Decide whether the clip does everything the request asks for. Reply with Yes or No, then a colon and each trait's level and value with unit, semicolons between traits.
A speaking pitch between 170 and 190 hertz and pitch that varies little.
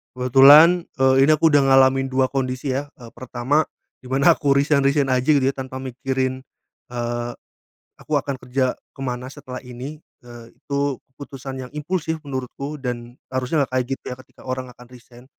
No: low, 130 Hz; narrow, 2.0 semitones